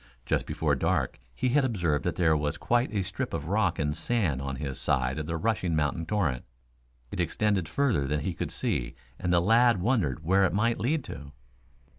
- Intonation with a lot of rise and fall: Yes, wide, 6.7 semitones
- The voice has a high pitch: No, very low, 85 Hz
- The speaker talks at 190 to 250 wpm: Yes, average, 200 wpm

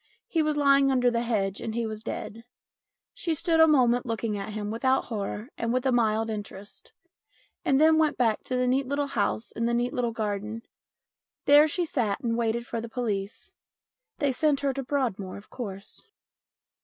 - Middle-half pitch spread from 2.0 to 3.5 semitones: No, average, 4.1 semitones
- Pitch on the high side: Yes, high, 235 Hz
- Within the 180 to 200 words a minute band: Yes, average, 190 wpm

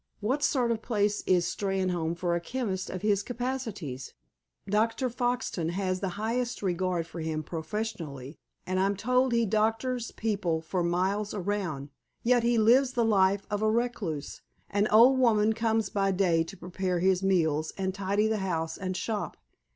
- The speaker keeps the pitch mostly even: No, average, 4.0 semitones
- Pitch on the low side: No, high, 200 Hz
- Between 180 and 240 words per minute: No, average, 165 wpm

